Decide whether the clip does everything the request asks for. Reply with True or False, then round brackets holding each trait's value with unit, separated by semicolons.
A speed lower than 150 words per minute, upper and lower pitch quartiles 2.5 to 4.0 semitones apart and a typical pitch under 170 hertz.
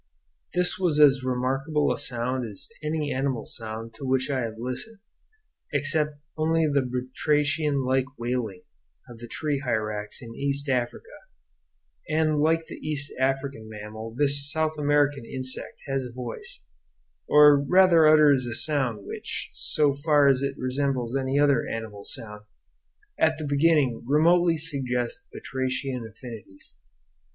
True (140 wpm; 3.4 semitones; 135 Hz)